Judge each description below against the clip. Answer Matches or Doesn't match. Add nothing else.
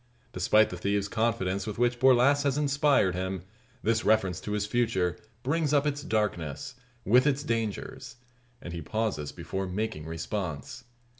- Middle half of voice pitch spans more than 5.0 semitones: Matches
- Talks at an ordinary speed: Matches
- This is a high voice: Doesn't match